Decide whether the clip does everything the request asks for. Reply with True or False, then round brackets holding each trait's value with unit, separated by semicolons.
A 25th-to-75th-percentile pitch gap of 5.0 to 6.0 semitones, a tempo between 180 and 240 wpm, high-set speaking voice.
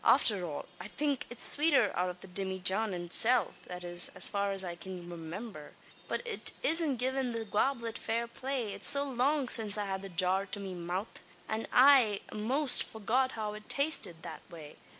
True (5.6 semitones; 190 wpm; 210 Hz)